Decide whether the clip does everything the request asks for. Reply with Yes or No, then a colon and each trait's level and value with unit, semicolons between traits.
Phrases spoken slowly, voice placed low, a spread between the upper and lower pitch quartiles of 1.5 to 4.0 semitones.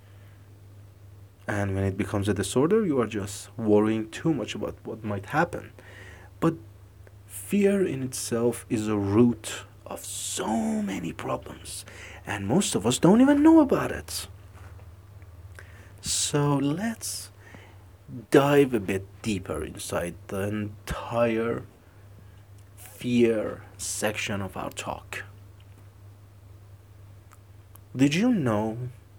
Yes: slow, 110 wpm; low, 100 Hz; narrow, 2.5 semitones